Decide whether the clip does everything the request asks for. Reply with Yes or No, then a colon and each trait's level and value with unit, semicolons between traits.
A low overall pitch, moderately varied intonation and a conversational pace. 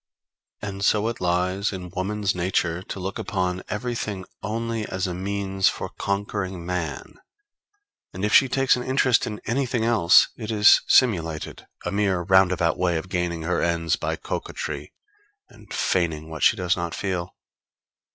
Yes: very low, 95 Hz; average, 3.1 semitones; average, 155 wpm